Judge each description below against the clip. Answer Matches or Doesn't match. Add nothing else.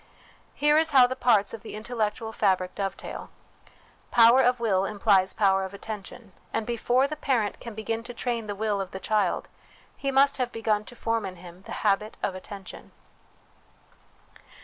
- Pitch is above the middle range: Matches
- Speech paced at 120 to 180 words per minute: Matches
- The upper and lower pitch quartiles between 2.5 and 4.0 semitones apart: Matches